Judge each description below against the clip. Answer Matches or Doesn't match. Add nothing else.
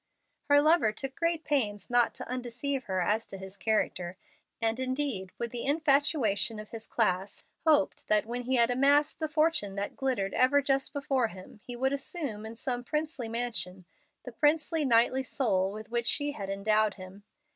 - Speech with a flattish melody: Doesn't match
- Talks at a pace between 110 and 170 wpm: Doesn't match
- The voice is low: Doesn't match